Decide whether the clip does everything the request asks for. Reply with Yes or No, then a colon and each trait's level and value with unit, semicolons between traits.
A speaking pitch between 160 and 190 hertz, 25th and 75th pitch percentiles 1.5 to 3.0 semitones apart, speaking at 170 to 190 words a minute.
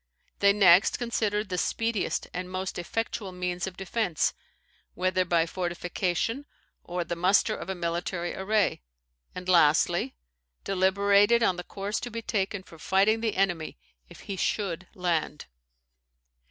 No: medium, 185 Hz; narrow, 2.6 semitones; average, 140 wpm